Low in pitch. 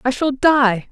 No: very high, 255 Hz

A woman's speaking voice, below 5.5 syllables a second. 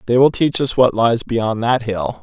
No: male; 4.4 syllables/s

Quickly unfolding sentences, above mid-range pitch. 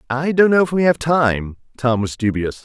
No: fast, 225 wpm; low, 135 Hz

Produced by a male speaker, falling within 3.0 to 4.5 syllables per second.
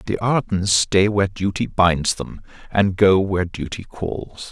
Yes: male; 4.2 syllables/s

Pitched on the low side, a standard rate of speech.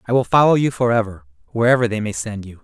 No: low, 110 Hz; fast, 250 wpm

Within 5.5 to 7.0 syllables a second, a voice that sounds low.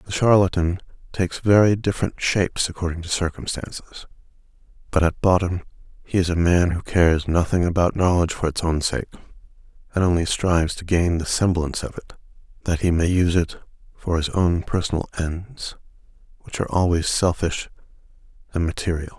Yes: 5.6 syllables/s; very low, 85 Hz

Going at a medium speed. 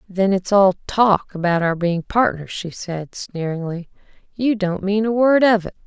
Yes: average, 185 wpm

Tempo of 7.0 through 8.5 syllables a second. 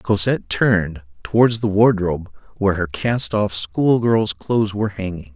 No: 4.9 syllables/s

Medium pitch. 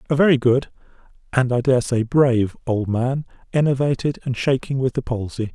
No: low, 130 Hz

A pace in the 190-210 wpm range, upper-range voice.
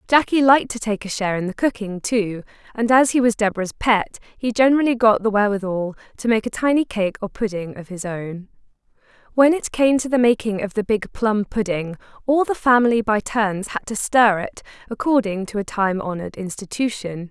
Yes: average, 200 wpm; high, 215 Hz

